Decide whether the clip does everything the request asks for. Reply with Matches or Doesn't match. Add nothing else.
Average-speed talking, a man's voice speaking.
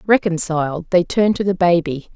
Doesn't match